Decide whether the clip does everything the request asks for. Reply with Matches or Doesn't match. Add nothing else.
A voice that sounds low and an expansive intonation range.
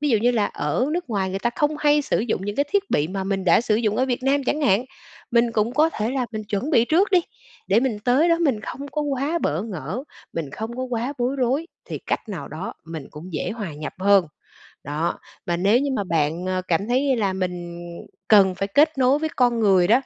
Doesn't match